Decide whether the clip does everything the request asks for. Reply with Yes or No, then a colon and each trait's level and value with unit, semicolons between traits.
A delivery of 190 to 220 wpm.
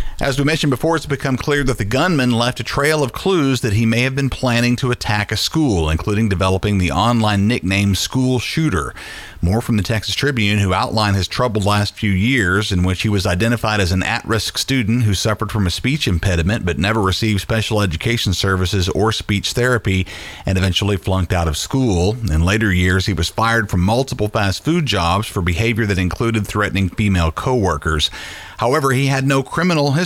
Yes: average, 200 wpm